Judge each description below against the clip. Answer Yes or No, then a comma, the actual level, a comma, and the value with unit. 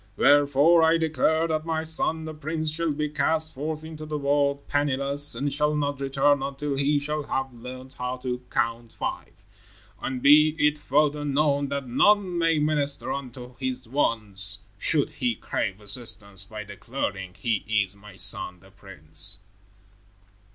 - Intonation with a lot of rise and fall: No, average, 3.9 semitones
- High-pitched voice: No, medium, 140 Hz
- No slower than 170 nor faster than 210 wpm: No, average, 155 wpm